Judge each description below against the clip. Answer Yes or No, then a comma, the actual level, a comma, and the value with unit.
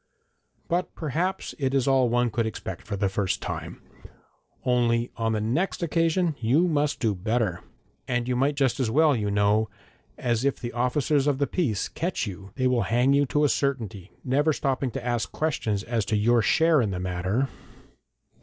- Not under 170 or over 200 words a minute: Yes, average, 185 wpm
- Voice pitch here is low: Yes, low, 125 Hz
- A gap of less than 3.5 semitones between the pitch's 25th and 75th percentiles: No, average, 4.5 semitones